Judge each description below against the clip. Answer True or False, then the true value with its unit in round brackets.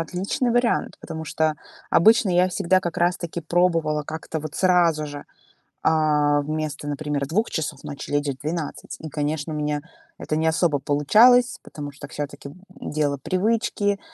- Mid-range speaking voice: True (155 Hz)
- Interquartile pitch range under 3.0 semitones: False (3.4 semitones)